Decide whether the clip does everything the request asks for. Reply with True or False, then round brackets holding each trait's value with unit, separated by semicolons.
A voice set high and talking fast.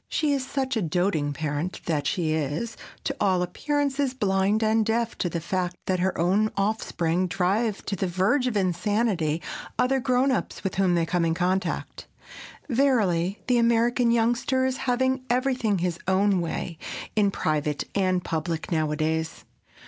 False (195 Hz; 155 wpm)